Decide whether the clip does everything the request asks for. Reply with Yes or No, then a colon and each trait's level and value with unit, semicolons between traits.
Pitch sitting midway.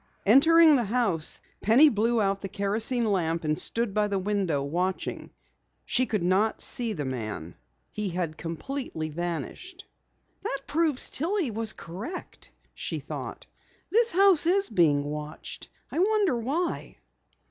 No: high, 215 Hz